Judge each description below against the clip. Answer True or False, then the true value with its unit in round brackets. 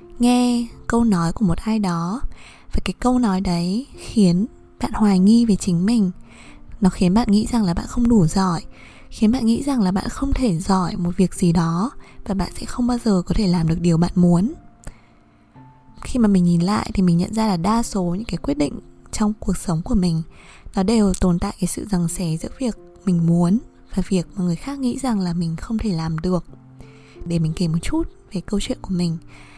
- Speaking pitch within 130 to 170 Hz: False (190 Hz)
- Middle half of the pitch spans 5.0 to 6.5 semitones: False (4.2 semitones)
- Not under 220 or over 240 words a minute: True (225 wpm)